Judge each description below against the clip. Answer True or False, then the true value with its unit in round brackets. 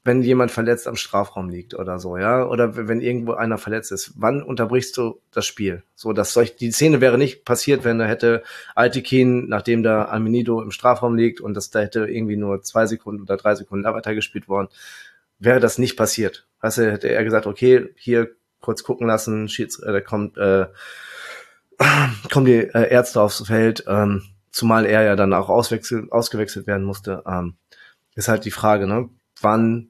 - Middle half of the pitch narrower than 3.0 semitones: True (2.6 semitones)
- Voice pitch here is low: True (110 Hz)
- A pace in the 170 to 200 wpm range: True (185 wpm)